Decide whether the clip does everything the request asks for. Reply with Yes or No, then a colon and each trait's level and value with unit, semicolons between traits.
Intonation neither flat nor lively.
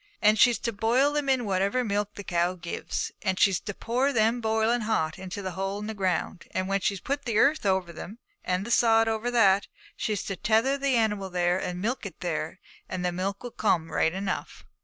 Yes: average, 3.7 semitones